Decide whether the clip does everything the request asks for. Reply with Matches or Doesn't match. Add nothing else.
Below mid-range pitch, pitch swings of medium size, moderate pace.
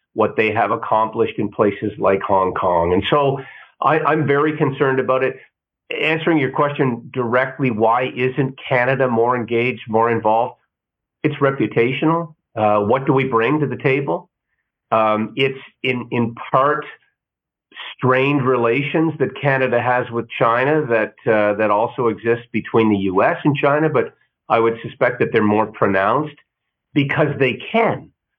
Matches